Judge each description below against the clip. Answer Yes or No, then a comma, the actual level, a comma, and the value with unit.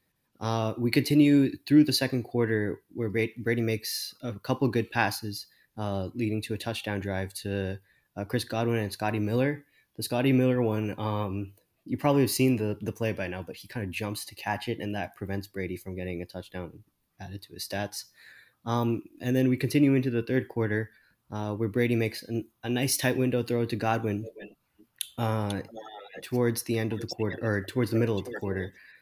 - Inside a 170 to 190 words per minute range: No, average, 200 wpm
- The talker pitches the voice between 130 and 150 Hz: No, low, 110 Hz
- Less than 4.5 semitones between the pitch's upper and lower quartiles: Yes, average, 2.8 semitones